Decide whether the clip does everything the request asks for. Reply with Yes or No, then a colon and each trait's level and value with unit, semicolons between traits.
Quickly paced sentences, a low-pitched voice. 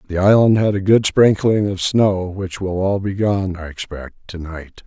Yes: fast, 210 wpm; very low, 95 Hz